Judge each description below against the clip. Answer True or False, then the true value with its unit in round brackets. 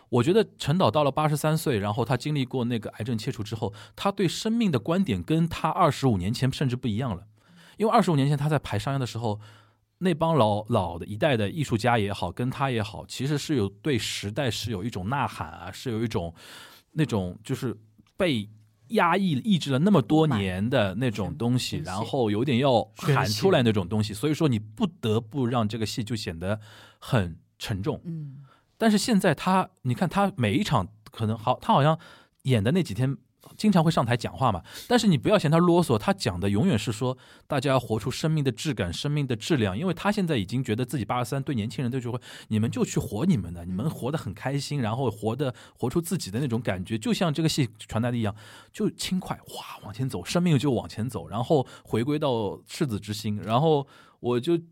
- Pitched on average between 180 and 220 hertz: False (125 Hz)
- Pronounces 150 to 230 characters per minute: False (320 characters per minute)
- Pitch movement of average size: False (6.1 semitones)